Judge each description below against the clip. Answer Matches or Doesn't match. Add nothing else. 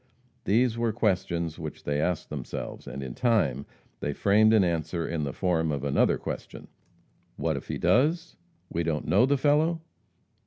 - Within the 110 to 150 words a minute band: Doesn't match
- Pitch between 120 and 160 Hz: Doesn't match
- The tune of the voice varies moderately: Doesn't match